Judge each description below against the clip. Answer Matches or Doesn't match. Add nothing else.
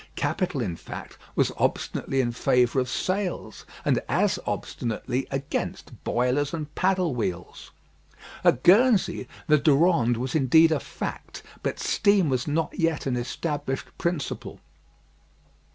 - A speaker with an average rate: Doesn't match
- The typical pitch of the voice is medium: Matches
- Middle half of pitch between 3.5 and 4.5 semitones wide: Doesn't match